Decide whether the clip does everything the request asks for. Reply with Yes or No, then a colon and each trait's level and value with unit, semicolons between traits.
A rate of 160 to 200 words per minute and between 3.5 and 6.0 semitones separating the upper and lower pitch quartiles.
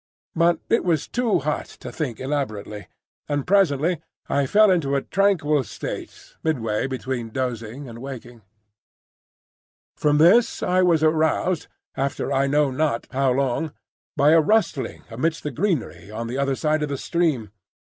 No: average, 150 wpm; average, 4.0 semitones